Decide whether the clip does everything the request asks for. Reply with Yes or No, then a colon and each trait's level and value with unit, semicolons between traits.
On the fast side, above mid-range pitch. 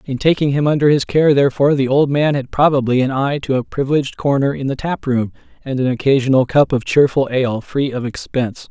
No: fast, 220 wpm; low, 135 Hz